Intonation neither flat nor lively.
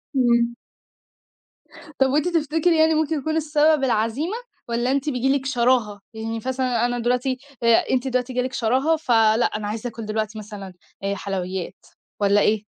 Yes: average, 3.8 semitones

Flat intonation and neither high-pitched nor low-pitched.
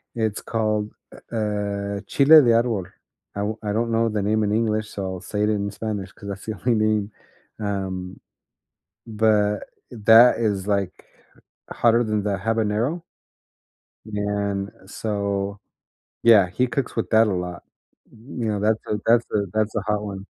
No: narrow, 1.8 semitones; low, 105 Hz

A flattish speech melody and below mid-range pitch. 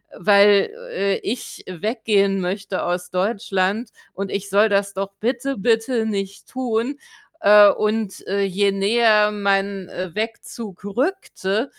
No: narrow, 2.3 semitones; high, 200 Hz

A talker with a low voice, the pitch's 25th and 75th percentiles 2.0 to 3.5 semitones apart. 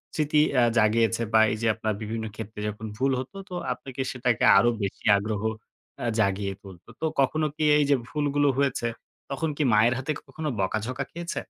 No: low, 120 Hz; average, 4.9 semitones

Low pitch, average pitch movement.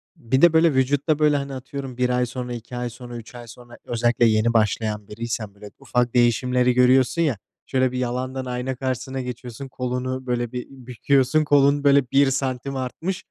No: low, 125 Hz; narrow, 1.9 semitones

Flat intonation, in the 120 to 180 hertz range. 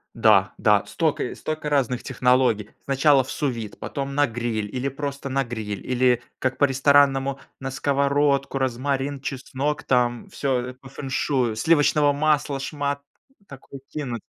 Yes: narrow, 2.1 semitones; low, 135 Hz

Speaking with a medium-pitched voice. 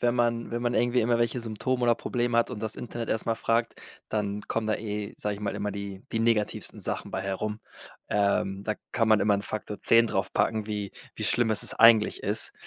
No: low, 110 Hz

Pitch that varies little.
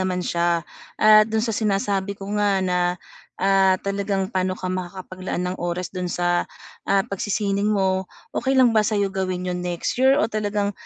Yes: narrow, 1.9 semitones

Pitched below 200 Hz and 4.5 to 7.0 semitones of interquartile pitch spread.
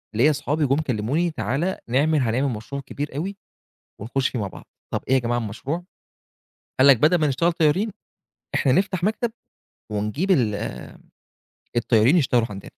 Yes: medium, 140 Hz; wide, 5.6 semitones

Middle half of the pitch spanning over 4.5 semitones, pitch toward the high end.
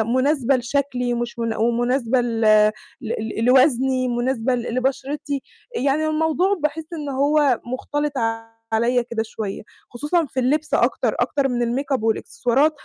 No: average, 3.3 semitones; very high, 255 Hz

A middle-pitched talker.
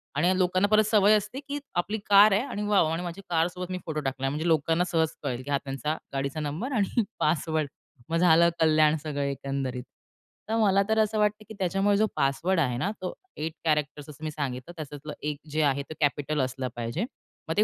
Yes: medium, 160 Hz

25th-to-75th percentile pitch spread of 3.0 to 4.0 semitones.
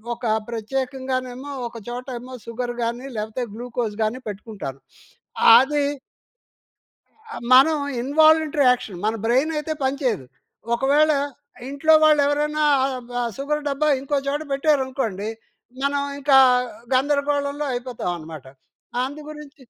Yes: average, 3.4 semitones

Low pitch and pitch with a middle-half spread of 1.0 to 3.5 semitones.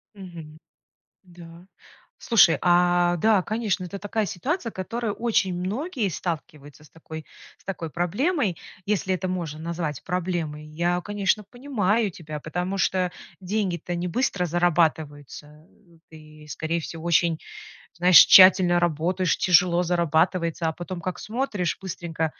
No: medium, 175 Hz; average, 3.0 semitones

